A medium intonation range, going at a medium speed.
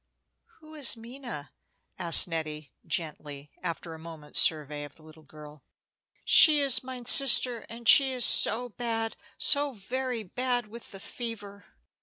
No: wide, 7.9 semitones; average, 145 wpm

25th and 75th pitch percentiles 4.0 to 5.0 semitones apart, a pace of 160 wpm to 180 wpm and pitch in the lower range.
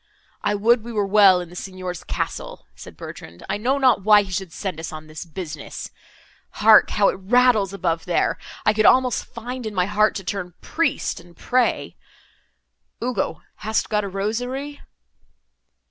No: average, 4.3 semitones; average, 170 wpm; high, 205 Hz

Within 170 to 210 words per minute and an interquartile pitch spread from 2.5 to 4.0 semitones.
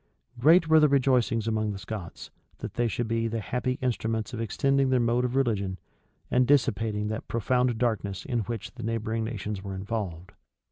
Yes: average, 180 wpm; average, 2.8 semitones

